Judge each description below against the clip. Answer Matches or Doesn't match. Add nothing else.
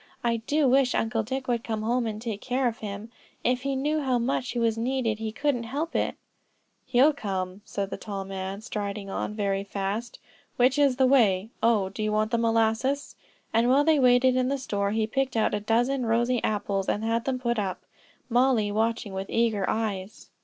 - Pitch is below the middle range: Doesn't match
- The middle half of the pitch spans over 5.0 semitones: Doesn't match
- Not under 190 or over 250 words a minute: Matches